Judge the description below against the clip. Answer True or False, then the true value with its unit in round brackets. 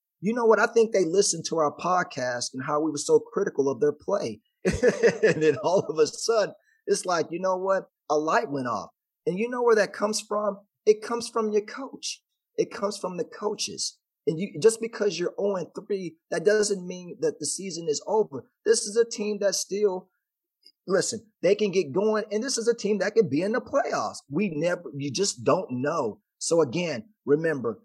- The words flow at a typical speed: False (210 wpm)